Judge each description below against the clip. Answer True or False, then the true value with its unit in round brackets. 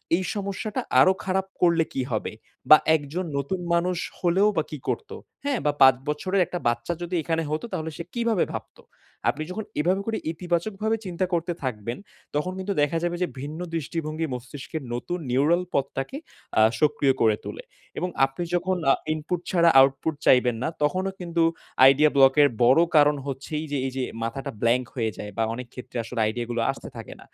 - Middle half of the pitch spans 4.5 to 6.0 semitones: True (5.2 semitones)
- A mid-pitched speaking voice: True (160 Hz)